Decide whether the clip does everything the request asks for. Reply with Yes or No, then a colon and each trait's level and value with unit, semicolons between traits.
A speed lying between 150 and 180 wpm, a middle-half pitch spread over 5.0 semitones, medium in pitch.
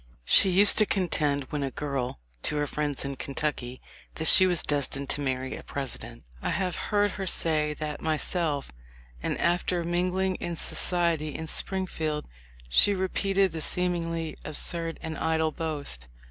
No: average, 155 wpm; average, 3.6 semitones; medium, 160 Hz